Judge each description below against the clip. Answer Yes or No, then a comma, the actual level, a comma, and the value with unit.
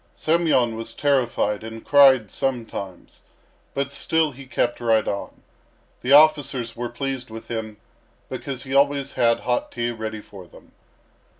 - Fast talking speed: No, average, 140 wpm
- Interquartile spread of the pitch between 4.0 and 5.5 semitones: No, average, 3.6 semitones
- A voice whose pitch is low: Yes, low, 120 Hz